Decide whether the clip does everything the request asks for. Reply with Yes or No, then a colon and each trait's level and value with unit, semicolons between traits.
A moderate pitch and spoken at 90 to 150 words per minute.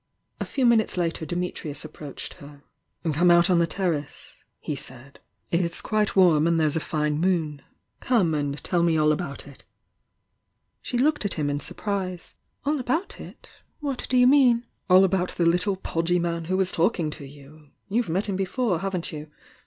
No: medium, 175 Hz; average, 175 wpm